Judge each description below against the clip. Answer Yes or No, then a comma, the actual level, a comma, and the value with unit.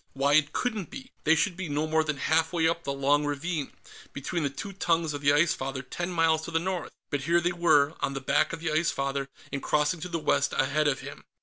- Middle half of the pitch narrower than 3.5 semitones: Yes, average, 3.1 semitones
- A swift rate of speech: Yes, fast, 250 wpm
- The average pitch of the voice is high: No, medium, 155 Hz